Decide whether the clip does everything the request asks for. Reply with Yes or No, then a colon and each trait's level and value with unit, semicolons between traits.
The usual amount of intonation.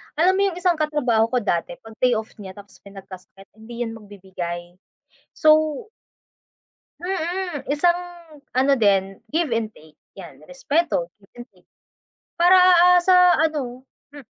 No: wide, 8.6 semitones